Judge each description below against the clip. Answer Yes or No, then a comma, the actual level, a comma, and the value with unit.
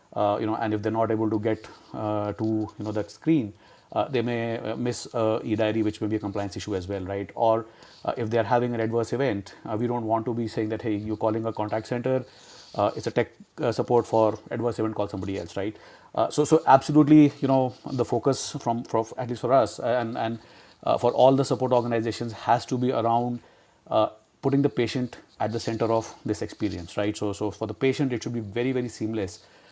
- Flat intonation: Yes, narrow, 2.2 semitones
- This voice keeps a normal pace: No, fast, 230 wpm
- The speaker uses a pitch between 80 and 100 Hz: No, low, 115 Hz